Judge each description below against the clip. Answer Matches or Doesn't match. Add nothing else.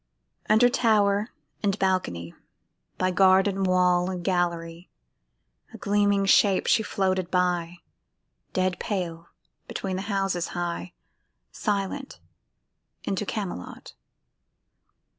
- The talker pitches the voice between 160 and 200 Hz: Matches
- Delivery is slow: Matches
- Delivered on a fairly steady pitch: Matches